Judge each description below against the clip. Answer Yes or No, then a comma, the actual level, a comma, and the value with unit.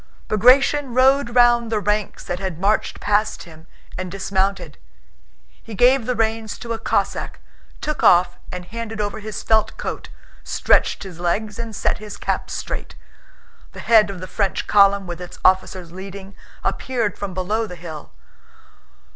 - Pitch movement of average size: Yes, average, 3.5 semitones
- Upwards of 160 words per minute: No, average, 155 wpm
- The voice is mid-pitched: No, high, 205 Hz